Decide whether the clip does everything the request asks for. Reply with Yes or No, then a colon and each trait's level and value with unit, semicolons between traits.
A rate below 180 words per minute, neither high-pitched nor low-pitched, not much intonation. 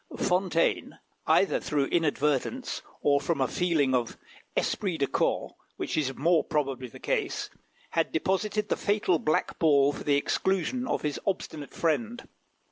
No: average, 145 wpm; medium, 160 Hz; average, 5.0 semitones